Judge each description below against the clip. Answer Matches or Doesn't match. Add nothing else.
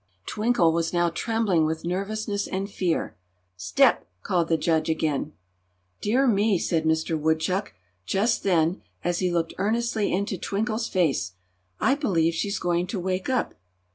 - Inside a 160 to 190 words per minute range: Doesn't match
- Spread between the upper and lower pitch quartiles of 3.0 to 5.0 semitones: Matches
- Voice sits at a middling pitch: Matches